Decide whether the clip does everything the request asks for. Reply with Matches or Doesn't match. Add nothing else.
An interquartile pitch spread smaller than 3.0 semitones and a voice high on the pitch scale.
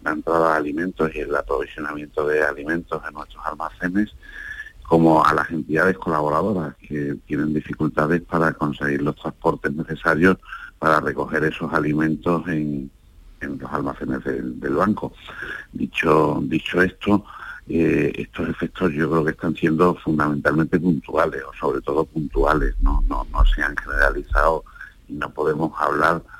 Doesn't match